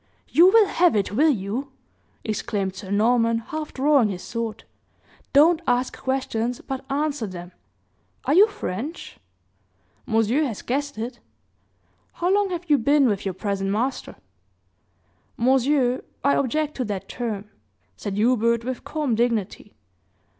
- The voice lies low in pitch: No, high, 245 Hz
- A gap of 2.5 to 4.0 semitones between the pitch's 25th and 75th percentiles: No, average, 5.3 semitones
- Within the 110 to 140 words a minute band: Yes, slow, 135 wpm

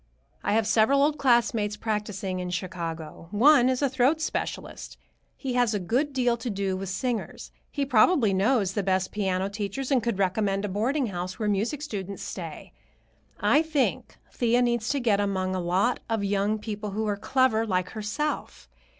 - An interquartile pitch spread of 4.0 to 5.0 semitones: Yes, average, 4.3 semitones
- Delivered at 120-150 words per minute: No, average, 175 wpm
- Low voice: No, high, 215 Hz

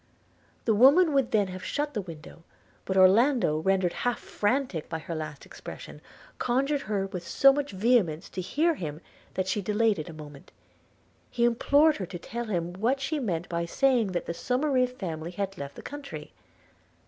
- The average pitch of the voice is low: No, high, 205 Hz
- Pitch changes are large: Yes, wide, 6.9 semitones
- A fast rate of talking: No, average, 185 wpm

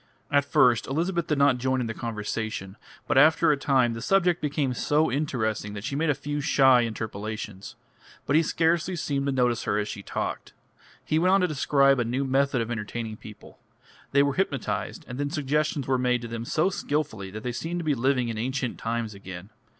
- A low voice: Yes, low, 130 Hz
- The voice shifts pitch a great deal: No, average, 4.4 semitones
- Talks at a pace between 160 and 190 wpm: No, fast, 205 wpm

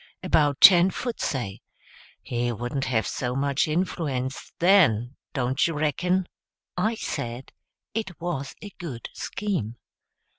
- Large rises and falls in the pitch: Yes, wide, 6.3 semitones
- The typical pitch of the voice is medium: Yes, medium, 145 Hz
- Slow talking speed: Yes, slow, 120 wpm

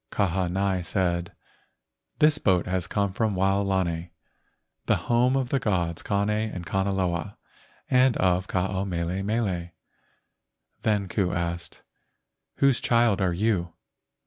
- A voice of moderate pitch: No, very low, 95 Hz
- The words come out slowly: Yes, slow, 130 wpm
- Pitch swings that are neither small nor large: Yes, average, 3.2 semitones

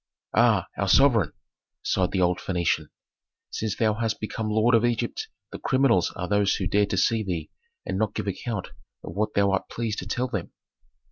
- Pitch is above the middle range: No, low, 105 Hz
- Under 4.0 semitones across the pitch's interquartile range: Yes, average, 3.3 semitones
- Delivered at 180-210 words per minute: Yes, average, 190 wpm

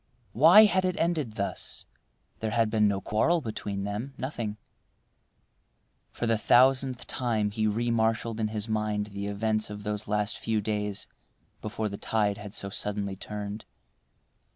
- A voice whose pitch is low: Yes, low, 110 Hz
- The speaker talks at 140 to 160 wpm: Yes, average, 150 wpm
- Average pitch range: No, narrow, 2.2 semitones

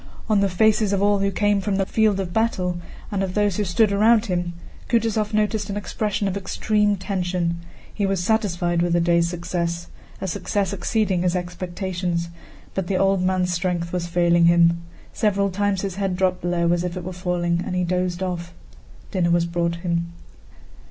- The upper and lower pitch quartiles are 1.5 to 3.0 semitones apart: Yes, narrow, 2.5 semitones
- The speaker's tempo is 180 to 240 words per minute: Yes, average, 185 wpm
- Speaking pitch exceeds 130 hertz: Yes, medium, 185 Hz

